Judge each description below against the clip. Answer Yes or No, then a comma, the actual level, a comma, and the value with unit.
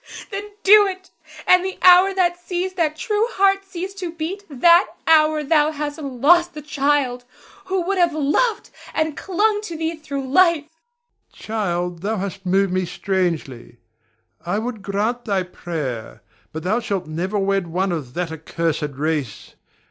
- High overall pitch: Yes, very high, 290 Hz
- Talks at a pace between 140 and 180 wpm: Yes, average, 160 wpm